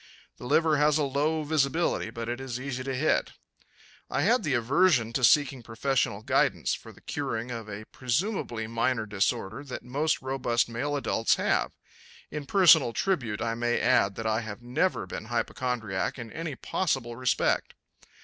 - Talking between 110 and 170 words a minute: Yes, average, 160 wpm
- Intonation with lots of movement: No, average, 4.1 semitones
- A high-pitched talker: No, low, 125 Hz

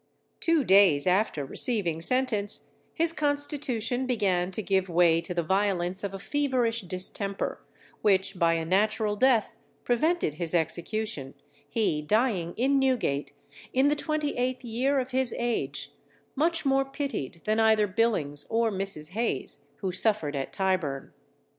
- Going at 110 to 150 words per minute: Yes, average, 140 wpm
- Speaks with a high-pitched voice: Yes, high, 210 Hz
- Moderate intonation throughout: No, wide, 6.3 semitones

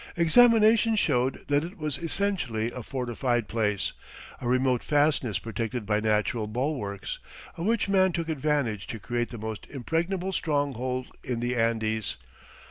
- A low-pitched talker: Yes, low, 130 Hz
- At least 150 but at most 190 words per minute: No, average, 140 wpm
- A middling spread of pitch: No, wide, 6.3 semitones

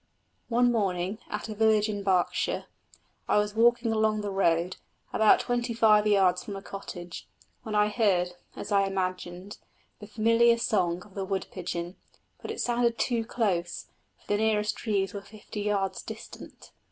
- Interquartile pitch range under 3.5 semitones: Yes, average, 2.7 semitones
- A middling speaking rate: Yes, average, 165 wpm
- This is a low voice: No, high, 205 Hz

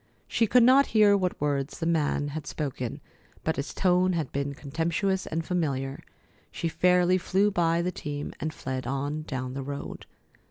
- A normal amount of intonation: Yes, average, 4.3 semitones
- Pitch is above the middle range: No, medium, 160 Hz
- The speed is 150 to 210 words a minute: Yes, average, 170 wpm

